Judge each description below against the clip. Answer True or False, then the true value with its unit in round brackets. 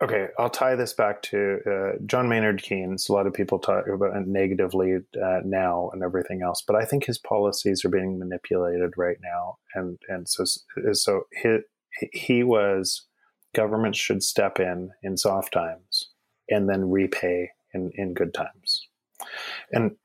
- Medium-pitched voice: False (95 Hz)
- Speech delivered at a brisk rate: False (160 wpm)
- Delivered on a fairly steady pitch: True (2.2 semitones)